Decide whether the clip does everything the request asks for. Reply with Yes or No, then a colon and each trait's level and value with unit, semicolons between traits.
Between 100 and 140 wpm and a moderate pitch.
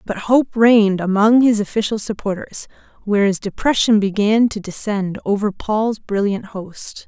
No: slow, 135 wpm; high, 210 Hz